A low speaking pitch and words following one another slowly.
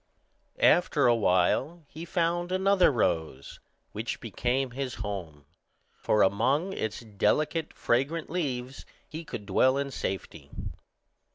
Yes: low, 130 Hz; slow, 115 wpm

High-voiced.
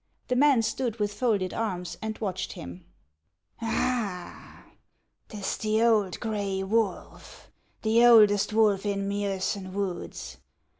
Yes: high, 205 Hz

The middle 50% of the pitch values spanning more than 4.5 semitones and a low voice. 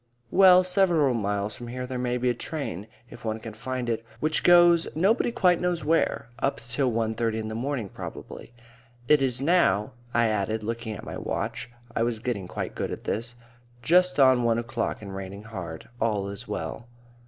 Yes: average, 5.3 semitones; low, 120 Hz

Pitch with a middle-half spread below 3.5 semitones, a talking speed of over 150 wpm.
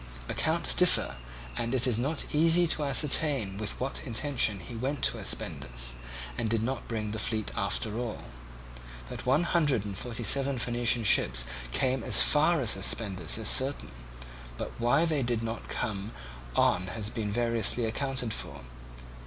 No: average, 4.1 semitones; average, 160 wpm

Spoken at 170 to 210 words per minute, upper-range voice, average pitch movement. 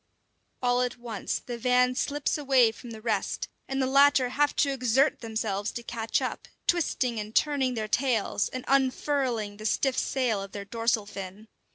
Yes: average, 175 wpm; high, 245 Hz; average, 3.4 semitones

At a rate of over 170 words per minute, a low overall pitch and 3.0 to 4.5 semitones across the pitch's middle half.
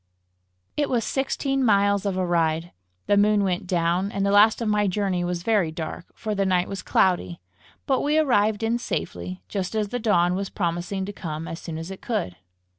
No: average, 200 wpm; high, 195 Hz; average, 3.5 semitones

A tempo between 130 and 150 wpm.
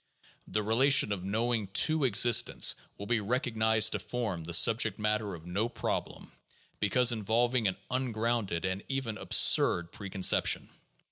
Yes: average, 140 wpm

